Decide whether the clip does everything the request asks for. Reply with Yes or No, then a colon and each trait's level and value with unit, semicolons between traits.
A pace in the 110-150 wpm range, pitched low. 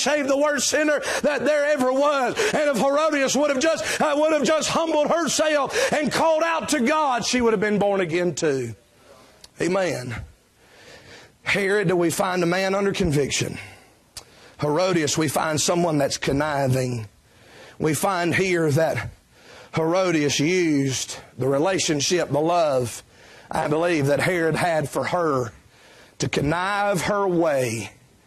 No: average, 140 wpm; medium, 180 Hz